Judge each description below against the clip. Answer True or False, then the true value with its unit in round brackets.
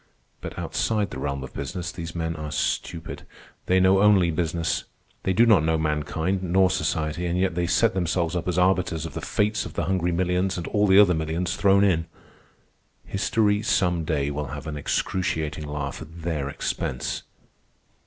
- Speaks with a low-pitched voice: True (85 Hz)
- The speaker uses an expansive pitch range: False (3.0 semitones)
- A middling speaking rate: True (180 wpm)